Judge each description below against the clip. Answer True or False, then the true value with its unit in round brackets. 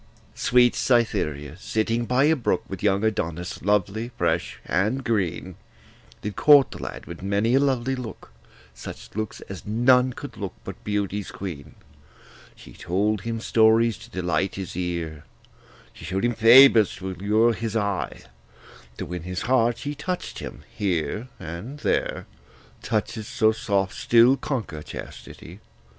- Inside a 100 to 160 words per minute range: True (145 wpm)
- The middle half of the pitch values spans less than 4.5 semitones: True (4.0 semitones)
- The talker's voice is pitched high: False (110 Hz)